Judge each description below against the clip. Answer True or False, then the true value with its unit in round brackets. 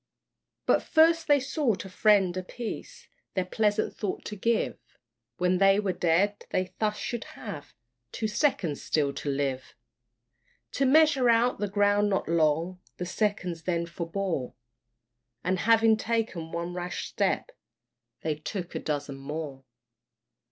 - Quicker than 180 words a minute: False (135 wpm)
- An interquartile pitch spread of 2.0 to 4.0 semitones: False (4.5 semitones)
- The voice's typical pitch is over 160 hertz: True (190 Hz)